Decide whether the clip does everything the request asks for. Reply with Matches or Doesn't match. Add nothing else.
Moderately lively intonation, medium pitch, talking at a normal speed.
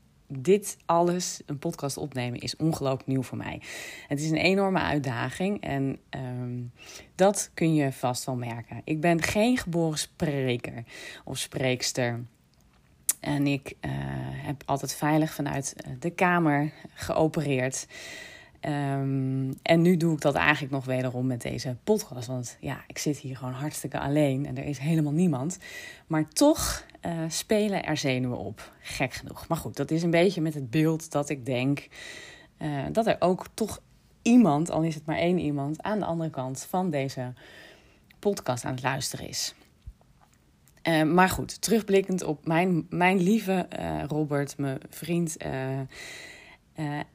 Matches